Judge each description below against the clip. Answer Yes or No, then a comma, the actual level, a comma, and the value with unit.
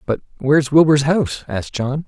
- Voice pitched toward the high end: No, medium, 145 Hz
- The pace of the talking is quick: No, average, 175 wpm